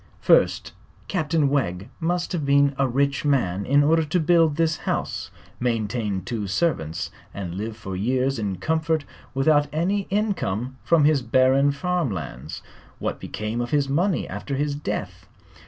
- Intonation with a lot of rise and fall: Yes, wide, 6.5 semitones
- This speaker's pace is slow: No, average, 155 wpm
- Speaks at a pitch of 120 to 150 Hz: Yes, medium, 140 Hz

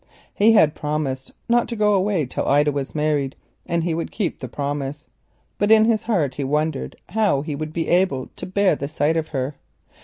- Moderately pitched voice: Yes, medium, 155 Hz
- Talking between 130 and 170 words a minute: No, average, 185 wpm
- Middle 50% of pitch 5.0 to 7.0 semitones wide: Yes, wide, 5.6 semitones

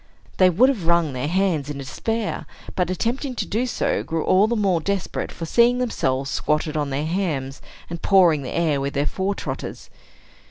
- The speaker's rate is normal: Yes, average, 190 wpm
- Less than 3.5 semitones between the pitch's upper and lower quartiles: No, average, 5.3 semitones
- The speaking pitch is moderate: Yes, medium, 170 Hz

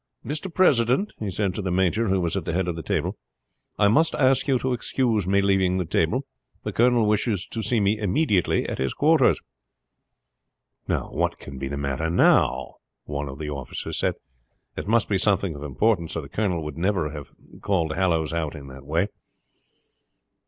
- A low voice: Yes, very low, 95 Hz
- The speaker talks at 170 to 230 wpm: Yes, average, 190 wpm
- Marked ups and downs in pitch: Yes, wide, 5.8 semitones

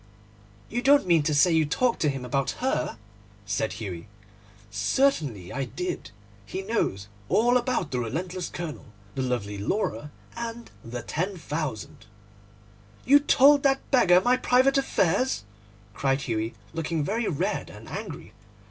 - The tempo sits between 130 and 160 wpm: Yes, average, 145 wpm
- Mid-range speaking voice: Yes, medium, 165 Hz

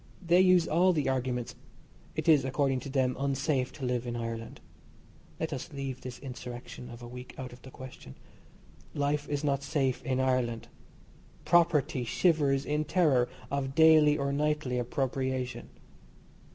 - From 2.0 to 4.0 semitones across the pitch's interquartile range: Yes, average, 2.9 semitones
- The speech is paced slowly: No, average, 150 wpm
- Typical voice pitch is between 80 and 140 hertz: Yes, low, 135 Hz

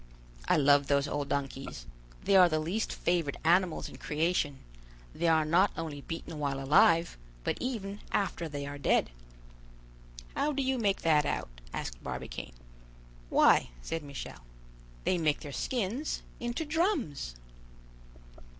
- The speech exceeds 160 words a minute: No, average, 140 wpm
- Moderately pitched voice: Yes, medium, 160 Hz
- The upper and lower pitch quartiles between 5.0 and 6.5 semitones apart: Yes, wide, 5.6 semitones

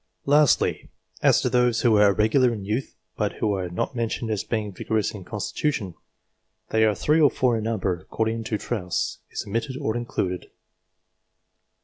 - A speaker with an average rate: Yes, average, 165 wpm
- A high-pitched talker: No, low, 110 Hz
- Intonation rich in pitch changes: No, average, 2.8 semitones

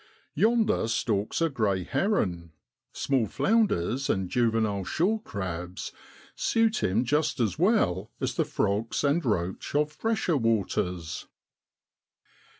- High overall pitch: No, low, 115 Hz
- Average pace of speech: No, slow, 110 wpm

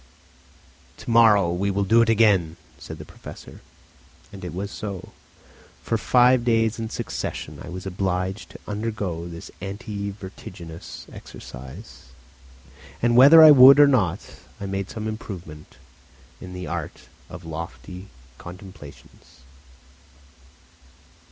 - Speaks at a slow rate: Yes, slow, 125 wpm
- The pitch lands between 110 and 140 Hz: No, low, 100 Hz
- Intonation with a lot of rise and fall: No, average, 4.0 semitones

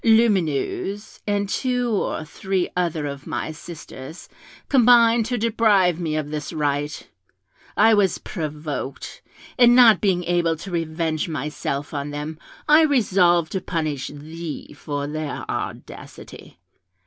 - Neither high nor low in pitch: Yes, medium, 170 Hz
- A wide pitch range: Yes, wide, 5.7 semitones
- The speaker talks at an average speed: No, slow, 125 wpm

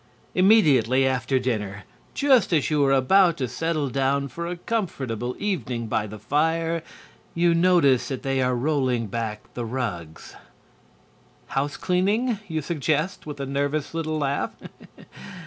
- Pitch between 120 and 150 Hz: Yes, medium, 140 Hz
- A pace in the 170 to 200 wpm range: No, average, 140 wpm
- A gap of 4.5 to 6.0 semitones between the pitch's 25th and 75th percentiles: Yes, average, 4.9 semitones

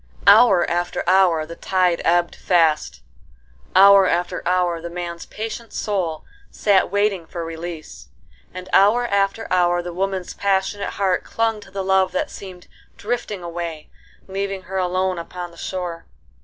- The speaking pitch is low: No, medium, 185 Hz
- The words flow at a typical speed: Yes, average, 145 wpm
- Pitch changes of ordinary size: No, narrow, 2.3 semitones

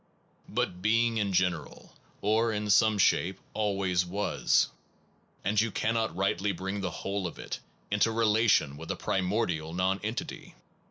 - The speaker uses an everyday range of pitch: Yes, average, 3.0 semitones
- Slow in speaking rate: No, average, 145 wpm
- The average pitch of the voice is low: Yes, low, 100 Hz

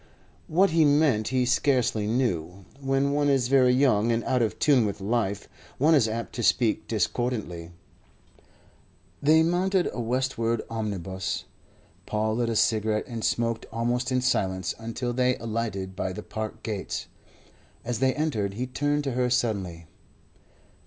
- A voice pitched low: Yes, low, 115 Hz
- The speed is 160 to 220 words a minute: No, average, 150 wpm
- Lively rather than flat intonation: No, average, 3.6 semitones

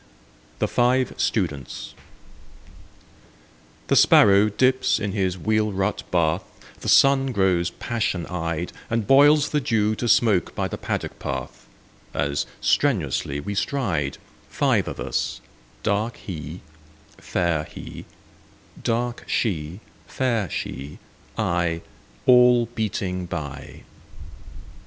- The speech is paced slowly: Yes, slow, 110 wpm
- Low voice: Yes, low, 100 Hz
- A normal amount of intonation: No, wide, 6.3 semitones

